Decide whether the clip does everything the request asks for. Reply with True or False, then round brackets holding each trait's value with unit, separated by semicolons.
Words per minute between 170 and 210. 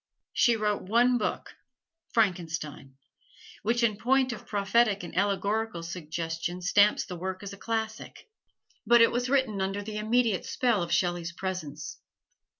False (140 wpm)